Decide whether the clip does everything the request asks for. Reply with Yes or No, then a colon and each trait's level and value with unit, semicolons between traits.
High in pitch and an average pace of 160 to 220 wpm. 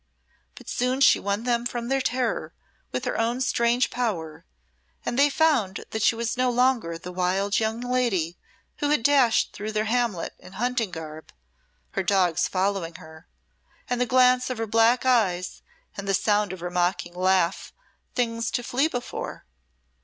Yes: high, 225 Hz; average, 170 wpm